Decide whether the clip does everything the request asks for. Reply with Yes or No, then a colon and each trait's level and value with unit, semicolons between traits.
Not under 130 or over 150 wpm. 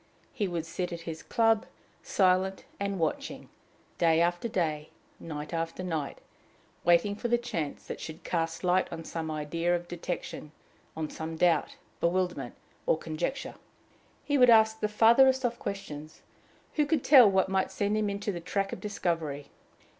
No: average, 160 wpm